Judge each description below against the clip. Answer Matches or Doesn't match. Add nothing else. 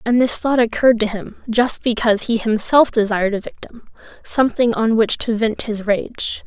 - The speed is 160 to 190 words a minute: Matches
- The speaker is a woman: Matches